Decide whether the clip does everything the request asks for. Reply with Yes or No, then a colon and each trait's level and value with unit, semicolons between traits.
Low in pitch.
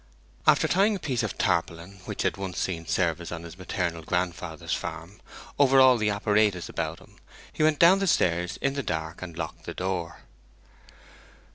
Yes: very low, 95 Hz